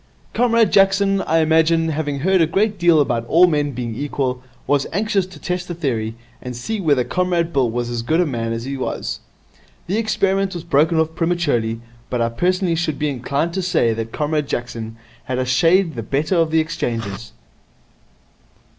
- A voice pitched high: No, medium, 155 Hz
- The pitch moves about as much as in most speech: No, wide, 6.0 semitones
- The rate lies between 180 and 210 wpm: Yes, average, 185 wpm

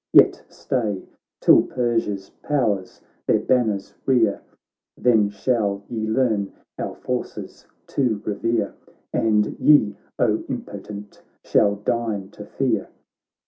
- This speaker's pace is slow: Yes, slow, 110 wpm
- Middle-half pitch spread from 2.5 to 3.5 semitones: Yes, average, 2.9 semitones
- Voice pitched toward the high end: No, low, 110 Hz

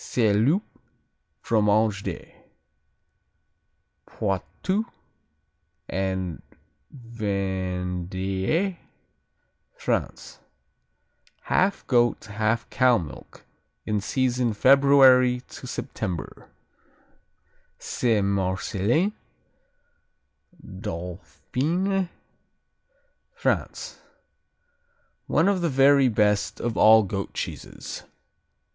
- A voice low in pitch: Yes, low, 110 Hz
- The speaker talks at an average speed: No, slow, 65 wpm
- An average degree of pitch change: No, wide, 5.7 semitones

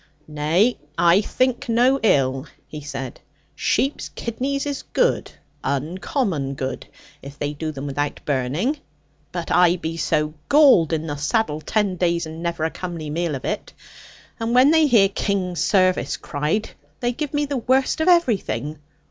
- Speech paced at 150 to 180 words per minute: Yes, average, 155 wpm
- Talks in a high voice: No, medium, 175 Hz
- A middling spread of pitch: No, wide, 8.3 semitones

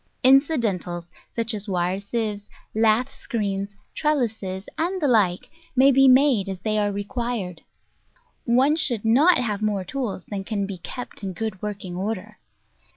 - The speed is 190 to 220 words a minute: No, average, 150 wpm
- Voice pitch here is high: Yes, high, 215 Hz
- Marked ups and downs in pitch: No, average, 4.3 semitones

